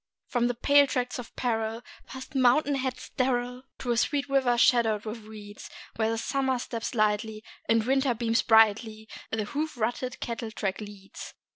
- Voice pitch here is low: No, high, 235 Hz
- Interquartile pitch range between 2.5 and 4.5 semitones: Yes, average, 2.8 semitones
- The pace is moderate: Yes, average, 160 wpm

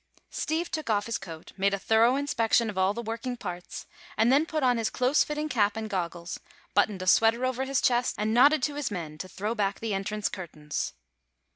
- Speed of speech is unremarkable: No, fast, 215 wpm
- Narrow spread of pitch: No, average, 4.5 semitones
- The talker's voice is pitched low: No, high, 225 Hz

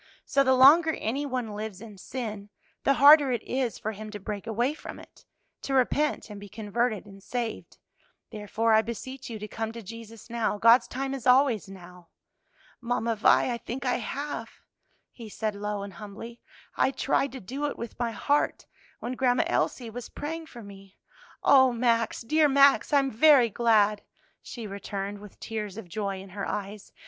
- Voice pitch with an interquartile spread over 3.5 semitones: Yes, average, 3.9 semitones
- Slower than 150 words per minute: No, average, 185 wpm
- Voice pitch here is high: Yes, high, 230 Hz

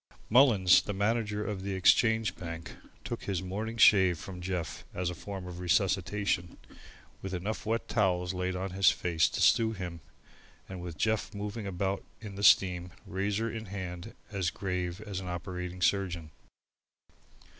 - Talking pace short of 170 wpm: Yes, average, 155 wpm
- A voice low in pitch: Yes, very low, 95 Hz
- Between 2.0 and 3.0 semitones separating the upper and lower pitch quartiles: Yes, narrow, 2.5 semitones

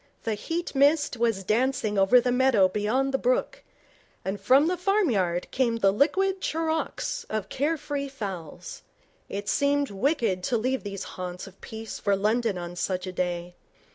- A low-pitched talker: No, high, 230 Hz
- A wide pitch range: Yes, wide, 6.5 semitones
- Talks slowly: No, average, 165 wpm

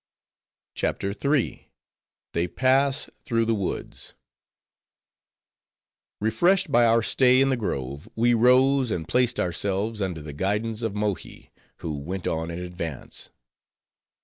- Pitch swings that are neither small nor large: No, wide, 6.0 semitones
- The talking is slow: Yes, slow, 120 wpm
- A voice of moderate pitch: No, low, 110 Hz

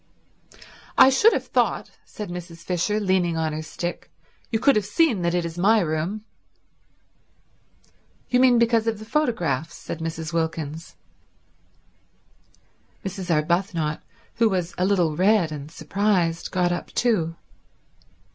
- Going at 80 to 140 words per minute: Yes, slow, 135 wpm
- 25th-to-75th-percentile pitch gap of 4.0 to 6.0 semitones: Yes, average, 4.6 semitones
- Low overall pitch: No, medium, 180 Hz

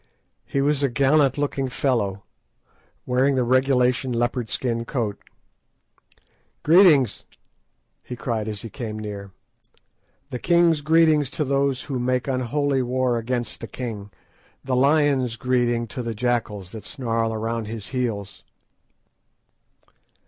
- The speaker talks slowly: Yes, slow, 120 wpm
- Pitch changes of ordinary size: Yes, average, 3.0 semitones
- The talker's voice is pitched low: Yes, low, 125 Hz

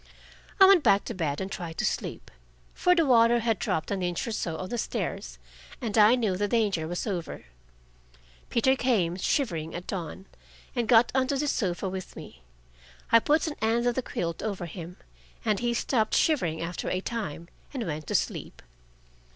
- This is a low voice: No, high, 210 Hz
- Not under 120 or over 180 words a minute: No, average, 190 wpm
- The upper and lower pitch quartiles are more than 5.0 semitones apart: Yes, wide, 5.5 semitones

